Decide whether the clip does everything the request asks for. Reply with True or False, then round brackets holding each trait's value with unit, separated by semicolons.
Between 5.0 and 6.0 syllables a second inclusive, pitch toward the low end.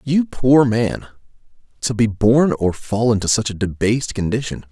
False (4.7 syllables/s; 115 Hz)